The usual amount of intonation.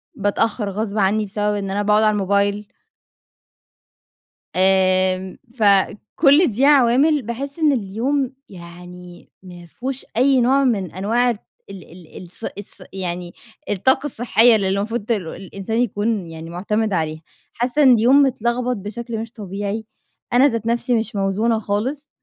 Yes: average, 4.0 semitones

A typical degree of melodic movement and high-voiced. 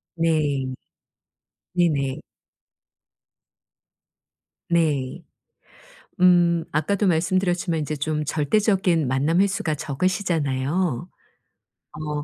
No: average, 3.4 semitones; medium, 160 Hz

